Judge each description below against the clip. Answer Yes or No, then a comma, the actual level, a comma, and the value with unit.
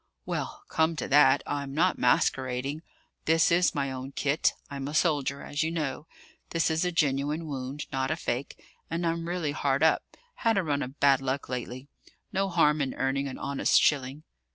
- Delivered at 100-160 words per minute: No, average, 185 wpm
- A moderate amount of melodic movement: Yes, average, 3.1 semitones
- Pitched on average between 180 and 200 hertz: No, medium, 145 Hz